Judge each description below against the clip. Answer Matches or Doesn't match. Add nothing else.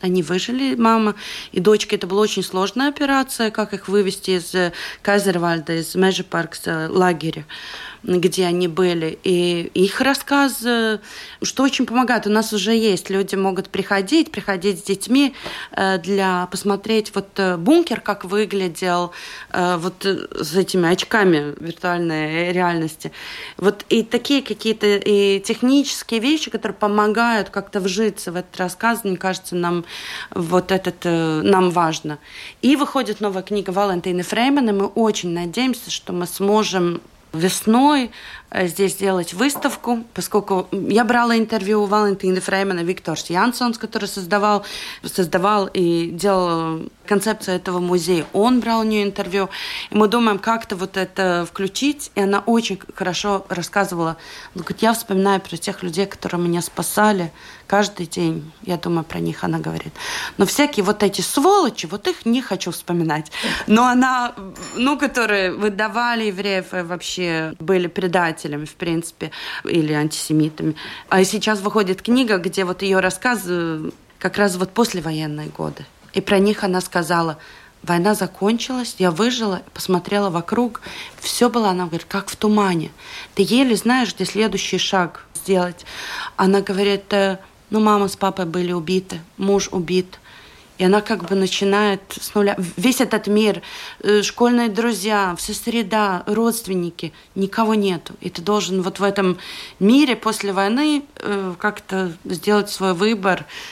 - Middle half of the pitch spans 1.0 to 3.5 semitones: Matches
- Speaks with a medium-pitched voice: Doesn't match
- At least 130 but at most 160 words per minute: Matches